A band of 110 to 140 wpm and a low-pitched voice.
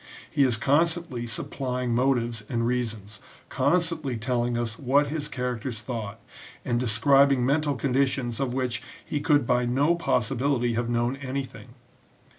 Yes: slow, 135 wpm; low, 125 Hz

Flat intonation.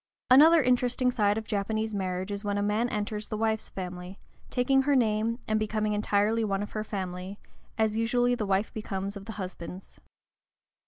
Yes: narrow, 2.3 semitones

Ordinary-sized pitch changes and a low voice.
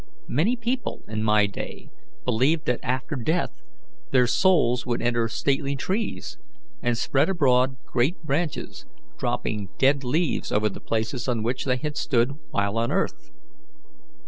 Yes: average, 4.5 semitones; low, 125 Hz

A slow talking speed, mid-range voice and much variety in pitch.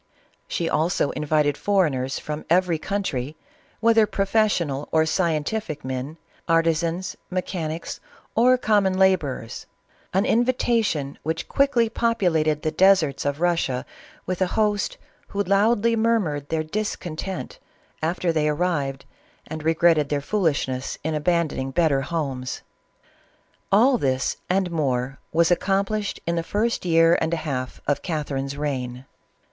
No: slow, 130 wpm; medium, 165 Hz; average, 4.9 semitones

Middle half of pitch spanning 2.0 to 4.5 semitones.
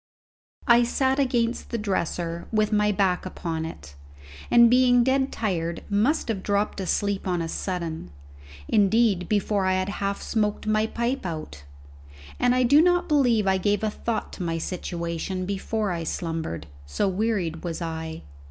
No: average, 5.3 semitones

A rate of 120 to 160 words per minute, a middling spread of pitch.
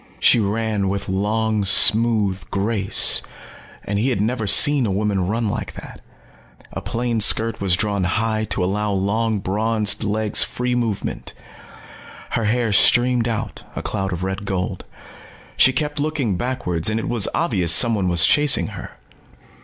Yes: average, 155 wpm; average, 3.0 semitones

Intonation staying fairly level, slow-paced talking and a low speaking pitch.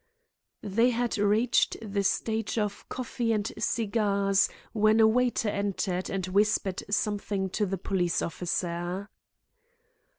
No: narrow, 2.3 semitones; slow, 120 wpm; high, 205 Hz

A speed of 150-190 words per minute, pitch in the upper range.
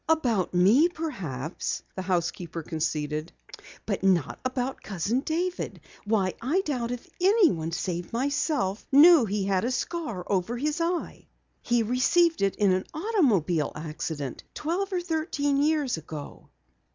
No: slow, 135 wpm; high, 235 Hz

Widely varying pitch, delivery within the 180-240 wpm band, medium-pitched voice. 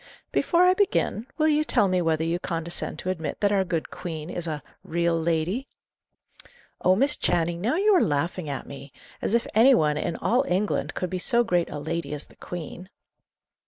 Yes: wide, 5.9 semitones; average, 195 wpm; medium, 175 Hz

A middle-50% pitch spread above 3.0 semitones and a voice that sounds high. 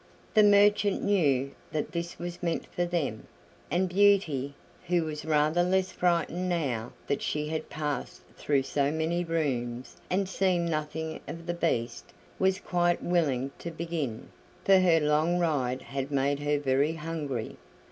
No: average, 3.8 semitones; medium, 160 Hz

